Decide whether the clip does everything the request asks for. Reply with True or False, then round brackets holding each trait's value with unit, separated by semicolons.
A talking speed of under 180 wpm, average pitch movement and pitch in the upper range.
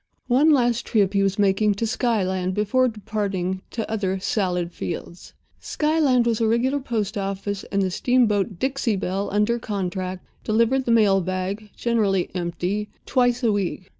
True (155 wpm; 3.7 semitones; 210 Hz)